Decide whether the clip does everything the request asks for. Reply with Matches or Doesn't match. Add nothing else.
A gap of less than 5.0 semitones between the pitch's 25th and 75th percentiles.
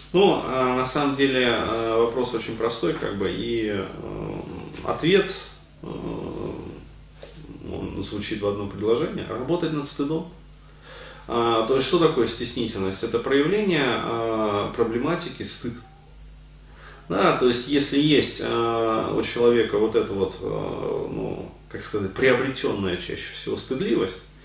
Matches